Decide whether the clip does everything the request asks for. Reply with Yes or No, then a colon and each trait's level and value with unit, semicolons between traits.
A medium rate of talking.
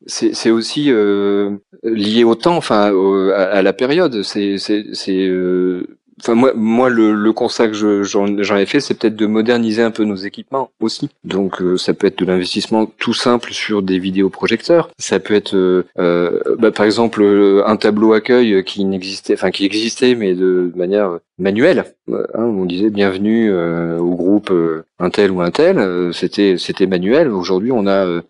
Yes: average, 195 wpm